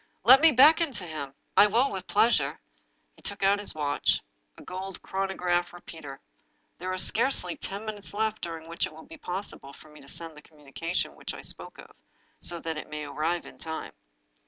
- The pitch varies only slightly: No, average, 4.8 semitones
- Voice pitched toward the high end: No, medium, 175 Hz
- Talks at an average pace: No, fast, 215 wpm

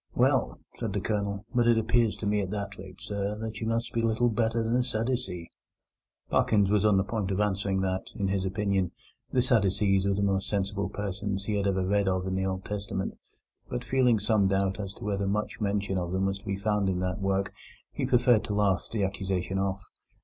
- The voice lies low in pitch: Yes, low, 100 Hz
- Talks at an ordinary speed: No, fast, 220 wpm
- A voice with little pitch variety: Yes, narrow, 1.9 semitones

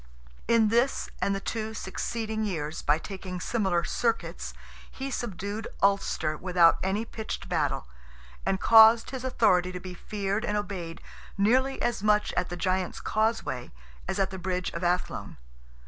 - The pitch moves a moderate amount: Yes, average, 3.6 semitones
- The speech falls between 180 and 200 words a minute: No, average, 150 wpm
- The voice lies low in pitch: No, high, 195 Hz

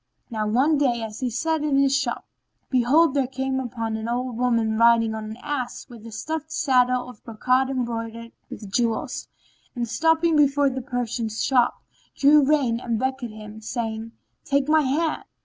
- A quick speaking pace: No, average, 170 wpm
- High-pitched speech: Yes, very high, 250 Hz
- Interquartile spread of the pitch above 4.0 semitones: No, average, 3.3 semitones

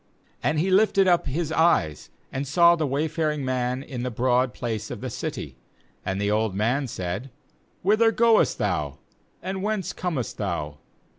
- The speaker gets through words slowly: No, average, 170 wpm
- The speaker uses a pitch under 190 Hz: Yes, low, 135 Hz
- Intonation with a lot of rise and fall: Yes, wide, 6.9 semitones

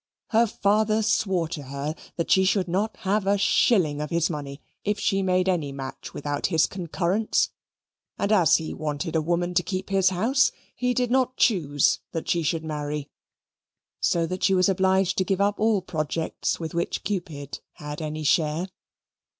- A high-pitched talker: No, medium, 180 Hz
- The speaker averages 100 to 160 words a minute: No, average, 175 wpm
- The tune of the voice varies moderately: Yes, average, 4.3 semitones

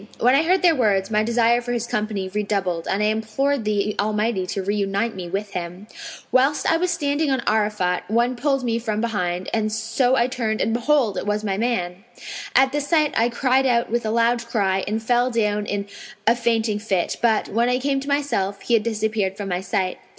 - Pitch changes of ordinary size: Yes, average, 3.2 semitones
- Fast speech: Yes, fast, 210 wpm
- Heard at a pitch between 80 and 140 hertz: No, high, 220 Hz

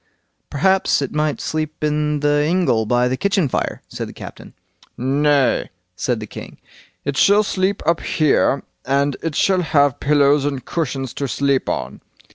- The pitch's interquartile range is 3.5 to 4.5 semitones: No, average, 2.7 semitones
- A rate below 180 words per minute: Yes, average, 160 wpm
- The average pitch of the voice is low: No, medium, 145 Hz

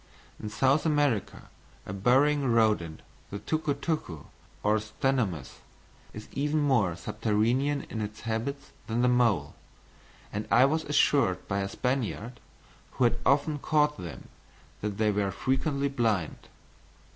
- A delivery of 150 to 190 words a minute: No, slow, 135 wpm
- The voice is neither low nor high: No, low, 120 Hz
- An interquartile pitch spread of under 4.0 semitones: No, average, 5.1 semitones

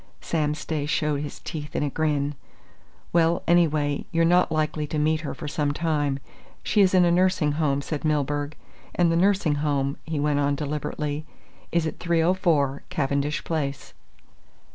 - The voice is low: No, medium, 150 Hz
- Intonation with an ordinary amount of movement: No, narrow, 2.3 semitones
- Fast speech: No, average, 165 wpm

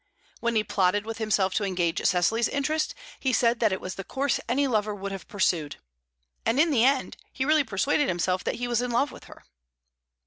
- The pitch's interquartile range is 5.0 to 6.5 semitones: Yes, average, 5.3 semitones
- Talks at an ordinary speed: No, fast, 210 wpm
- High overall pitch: Yes, high, 225 Hz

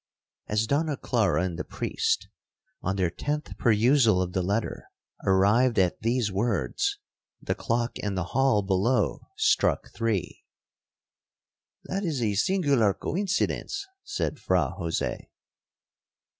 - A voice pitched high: No, low, 115 Hz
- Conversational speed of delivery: No, slow, 120 wpm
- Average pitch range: No, wide, 6.9 semitones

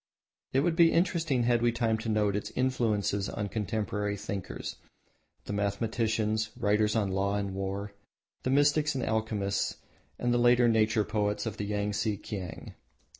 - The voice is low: Yes, low, 110 Hz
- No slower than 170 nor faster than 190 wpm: No, average, 155 wpm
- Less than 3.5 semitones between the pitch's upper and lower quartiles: Yes, average, 2.8 semitones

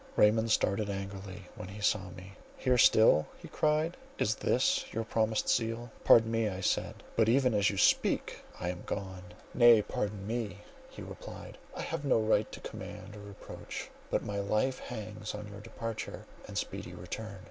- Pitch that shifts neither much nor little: No, narrow, 2.3 semitones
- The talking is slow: No, average, 175 wpm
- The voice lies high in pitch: No, low, 105 Hz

